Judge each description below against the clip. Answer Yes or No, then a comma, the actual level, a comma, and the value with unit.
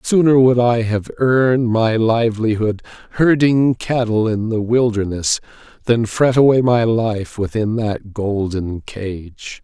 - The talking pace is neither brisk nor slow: No, slow, 130 wpm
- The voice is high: No, low, 115 Hz